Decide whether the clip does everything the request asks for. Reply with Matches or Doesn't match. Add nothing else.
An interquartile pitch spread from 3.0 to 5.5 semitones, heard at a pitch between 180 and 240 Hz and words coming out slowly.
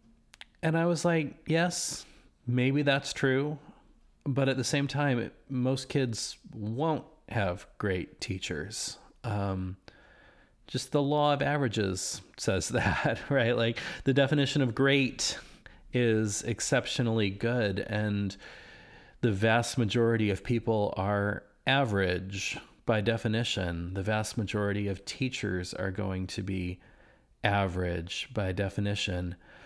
Doesn't match